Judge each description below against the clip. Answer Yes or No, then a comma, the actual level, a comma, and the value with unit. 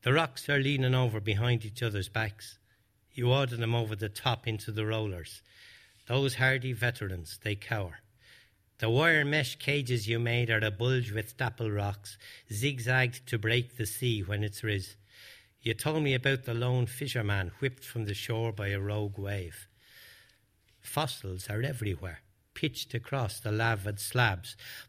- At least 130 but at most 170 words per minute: Yes, average, 160 wpm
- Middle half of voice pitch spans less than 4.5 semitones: Yes, average, 3.3 semitones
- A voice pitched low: Yes, low, 115 Hz